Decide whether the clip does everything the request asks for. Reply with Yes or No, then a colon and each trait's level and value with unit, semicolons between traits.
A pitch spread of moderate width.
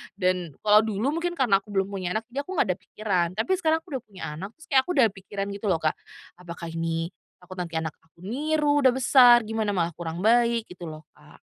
No: wide, 6.2 semitones